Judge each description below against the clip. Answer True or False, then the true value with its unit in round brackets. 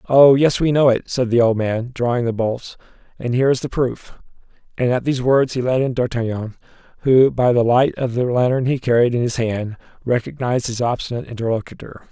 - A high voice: False (125 Hz)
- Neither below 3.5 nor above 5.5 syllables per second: False (5.8 syllables/s)